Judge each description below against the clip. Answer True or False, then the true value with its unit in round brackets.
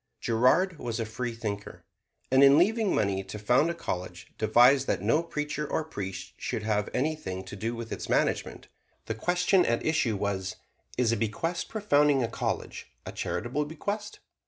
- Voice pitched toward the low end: True (125 Hz)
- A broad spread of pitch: True (6.4 semitones)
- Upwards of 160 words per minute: True (170 wpm)